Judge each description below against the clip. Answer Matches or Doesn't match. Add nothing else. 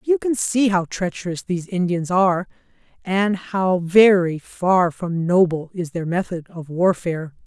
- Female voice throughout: Matches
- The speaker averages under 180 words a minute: Matches